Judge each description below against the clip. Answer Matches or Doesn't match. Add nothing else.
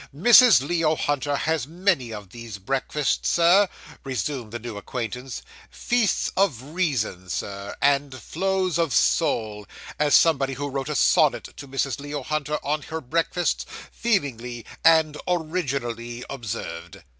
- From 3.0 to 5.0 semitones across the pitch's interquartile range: Doesn't match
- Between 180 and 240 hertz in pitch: Doesn't match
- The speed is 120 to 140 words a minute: Matches